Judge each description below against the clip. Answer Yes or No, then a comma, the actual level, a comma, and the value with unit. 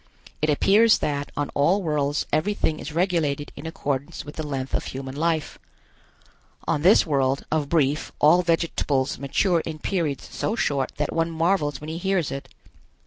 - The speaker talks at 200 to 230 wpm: No, average, 165 wpm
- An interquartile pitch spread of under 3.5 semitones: Yes, average, 3.0 semitones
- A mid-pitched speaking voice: Yes, medium, 155 Hz